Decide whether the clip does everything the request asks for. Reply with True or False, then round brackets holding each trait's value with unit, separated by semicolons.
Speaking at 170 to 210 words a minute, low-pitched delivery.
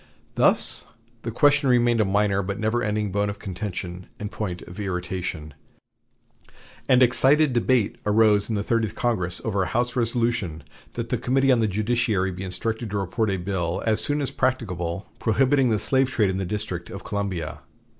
True (175 wpm; 105 Hz)